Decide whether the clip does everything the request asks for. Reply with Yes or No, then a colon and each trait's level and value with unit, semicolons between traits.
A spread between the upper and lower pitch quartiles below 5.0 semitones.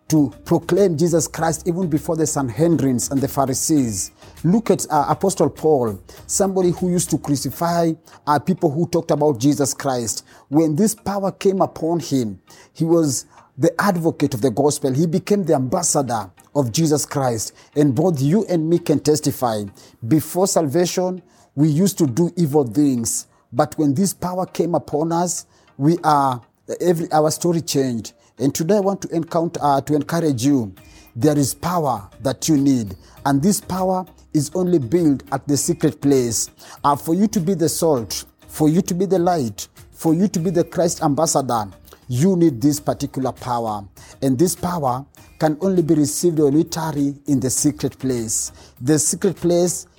Yes: average, 4.2 semitones